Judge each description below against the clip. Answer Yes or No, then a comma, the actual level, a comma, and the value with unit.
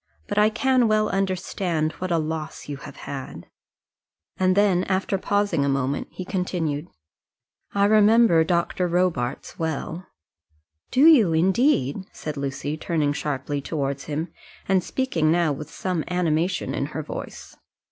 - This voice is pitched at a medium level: Yes, medium, 170 Hz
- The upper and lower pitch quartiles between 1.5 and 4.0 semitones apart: No, average, 4.4 semitones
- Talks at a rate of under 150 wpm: Yes, average, 140 wpm